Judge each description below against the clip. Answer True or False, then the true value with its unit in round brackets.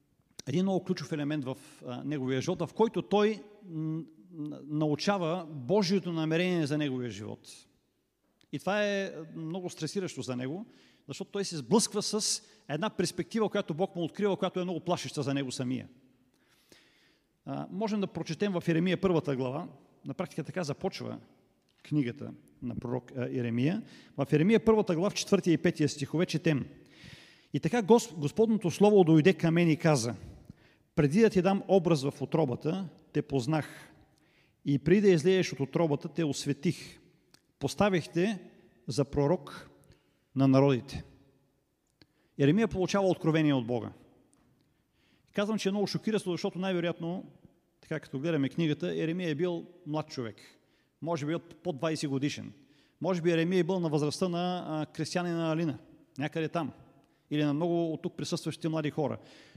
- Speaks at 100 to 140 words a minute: False (150 wpm)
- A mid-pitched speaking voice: True (165 Hz)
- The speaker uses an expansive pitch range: False (4.2 semitones)